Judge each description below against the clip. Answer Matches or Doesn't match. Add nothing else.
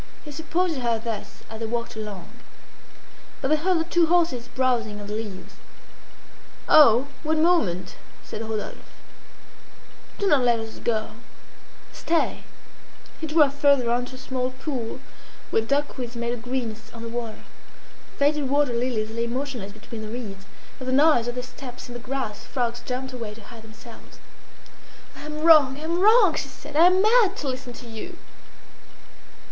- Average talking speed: Matches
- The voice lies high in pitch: Matches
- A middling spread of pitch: Matches